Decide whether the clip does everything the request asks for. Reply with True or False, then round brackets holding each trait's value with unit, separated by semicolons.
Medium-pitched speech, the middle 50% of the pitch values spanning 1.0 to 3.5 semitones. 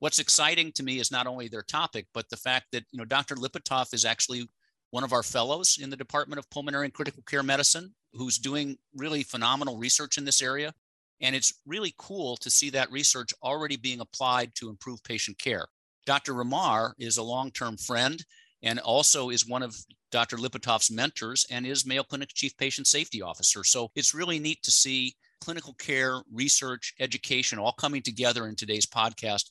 False (130 Hz; 2.9 semitones)